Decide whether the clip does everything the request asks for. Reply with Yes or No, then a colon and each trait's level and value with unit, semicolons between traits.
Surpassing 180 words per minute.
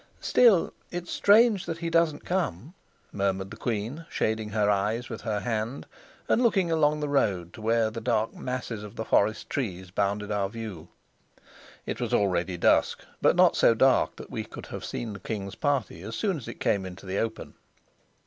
Yes: average, 190 wpm